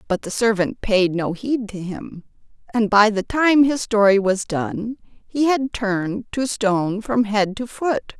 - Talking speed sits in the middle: Yes, average, 185 wpm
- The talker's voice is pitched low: No, high, 215 Hz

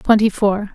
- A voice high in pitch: Yes, high, 205 Hz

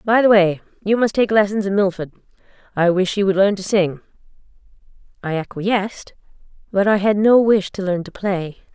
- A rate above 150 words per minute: Yes, average, 185 wpm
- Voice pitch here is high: Yes, high, 195 Hz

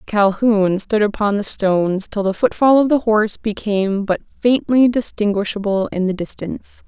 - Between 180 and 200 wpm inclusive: No, average, 155 wpm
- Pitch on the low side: No, high, 210 Hz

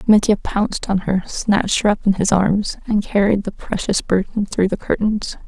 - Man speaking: No, female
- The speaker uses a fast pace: No, average, 195 wpm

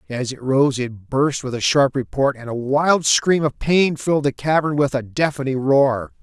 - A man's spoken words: Yes, male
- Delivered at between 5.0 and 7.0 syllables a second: No, 4.5 syllables/s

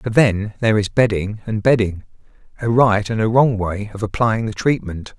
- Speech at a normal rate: Yes, average, 185 wpm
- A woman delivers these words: No, male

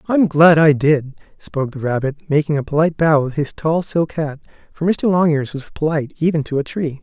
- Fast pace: Yes, fast, 220 wpm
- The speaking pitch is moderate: Yes, medium, 150 Hz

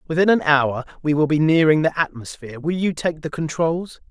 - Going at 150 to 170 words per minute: No, fast, 205 wpm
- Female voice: No, male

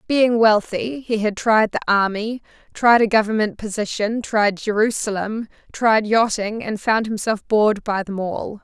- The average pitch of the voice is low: No, high, 215 Hz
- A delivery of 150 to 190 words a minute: Yes, average, 155 wpm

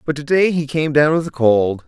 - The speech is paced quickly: Yes, fast, 255 wpm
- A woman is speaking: No, male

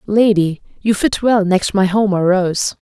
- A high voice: Yes, high, 200 Hz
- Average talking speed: Yes, average, 165 wpm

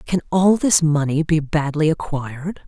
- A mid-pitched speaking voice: Yes, medium, 160 Hz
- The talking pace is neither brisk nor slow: Yes, average, 155 wpm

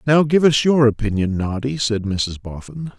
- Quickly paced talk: No, average, 180 wpm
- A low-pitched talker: Yes, low, 120 Hz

